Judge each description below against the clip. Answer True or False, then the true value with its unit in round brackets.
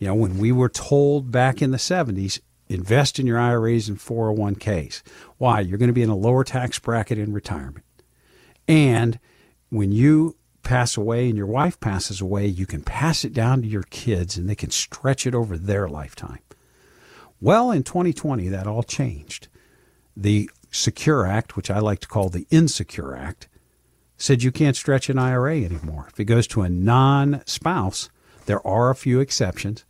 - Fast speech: False (180 wpm)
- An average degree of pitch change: True (4.3 semitones)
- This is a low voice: True (115 Hz)